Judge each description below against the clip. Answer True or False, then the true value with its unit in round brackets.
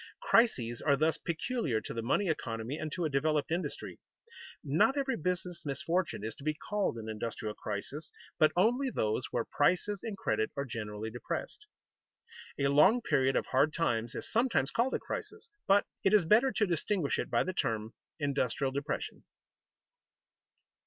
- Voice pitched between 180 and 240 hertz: False (155 Hz)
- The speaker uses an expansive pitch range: True (8.2 semitones)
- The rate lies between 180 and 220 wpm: False (165 wpm)